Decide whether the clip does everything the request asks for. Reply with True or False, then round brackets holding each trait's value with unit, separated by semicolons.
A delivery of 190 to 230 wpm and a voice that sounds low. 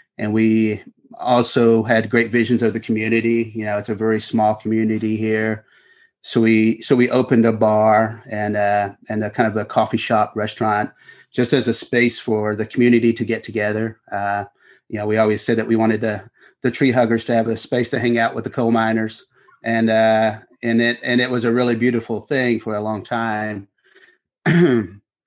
True (195 wpm; 115 Hz)